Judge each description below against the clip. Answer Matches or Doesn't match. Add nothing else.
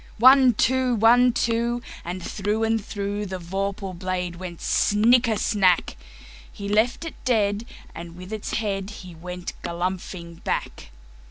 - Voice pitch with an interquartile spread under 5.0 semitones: Matches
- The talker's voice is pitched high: Matches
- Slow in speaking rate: Matches